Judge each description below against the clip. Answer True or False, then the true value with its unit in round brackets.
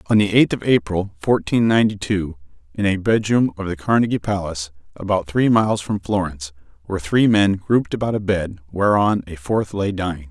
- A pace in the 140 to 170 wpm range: False (185 wpm)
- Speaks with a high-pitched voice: False (95 Hz)